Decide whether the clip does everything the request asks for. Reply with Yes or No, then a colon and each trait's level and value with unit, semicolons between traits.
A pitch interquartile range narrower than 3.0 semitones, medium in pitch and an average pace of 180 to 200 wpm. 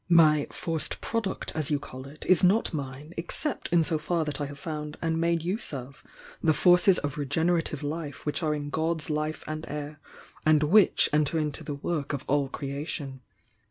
Yes: narrow, 2.4 semitones; medium, 155 Hz; average, 190 wpm